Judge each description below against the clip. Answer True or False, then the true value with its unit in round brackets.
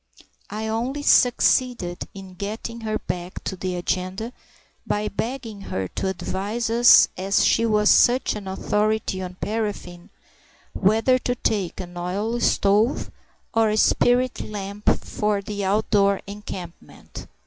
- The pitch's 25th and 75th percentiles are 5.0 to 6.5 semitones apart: False (3.1 semitones)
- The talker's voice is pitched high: True (210 Hz)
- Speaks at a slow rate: True (130 wpm)